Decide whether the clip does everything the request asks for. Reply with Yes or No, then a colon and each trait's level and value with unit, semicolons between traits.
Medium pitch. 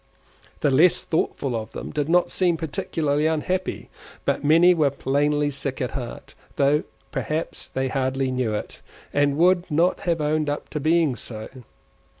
Yes: medium, 150 Hz